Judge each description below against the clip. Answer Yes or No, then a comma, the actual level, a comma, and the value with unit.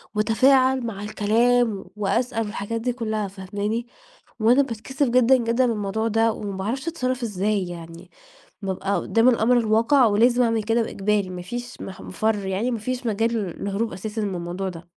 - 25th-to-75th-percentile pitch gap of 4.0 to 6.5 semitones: No, average, 3.2 semitones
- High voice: Yes, high, 220 Hz